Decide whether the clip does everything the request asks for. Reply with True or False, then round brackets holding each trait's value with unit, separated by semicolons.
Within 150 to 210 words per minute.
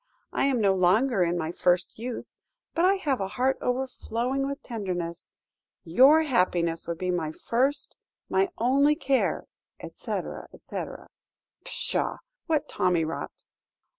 False (135 wpm)